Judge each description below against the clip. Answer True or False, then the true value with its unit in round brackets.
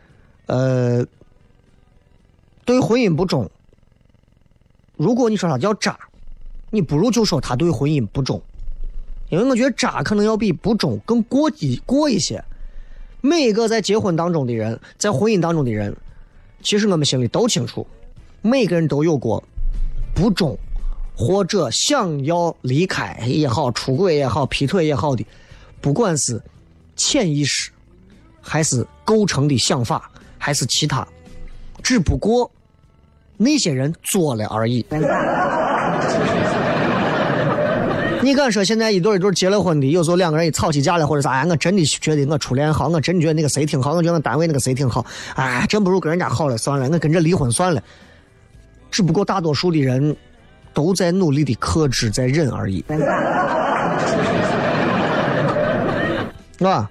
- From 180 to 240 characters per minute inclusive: True (225 characters per minute)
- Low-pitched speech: False (150 Hz)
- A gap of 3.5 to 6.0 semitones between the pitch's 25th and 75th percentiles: False (7.3 semitones)